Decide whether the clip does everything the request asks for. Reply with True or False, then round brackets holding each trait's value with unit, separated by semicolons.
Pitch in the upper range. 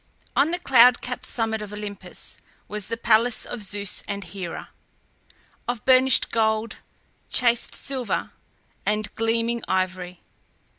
True (220 Hz)